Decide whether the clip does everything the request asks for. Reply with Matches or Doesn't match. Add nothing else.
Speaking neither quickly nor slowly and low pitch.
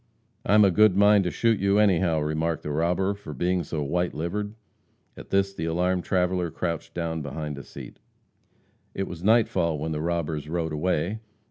Matches